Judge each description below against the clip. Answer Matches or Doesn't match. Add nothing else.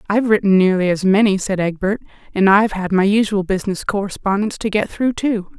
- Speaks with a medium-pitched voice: Doesn't match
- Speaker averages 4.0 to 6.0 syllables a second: Doesn't match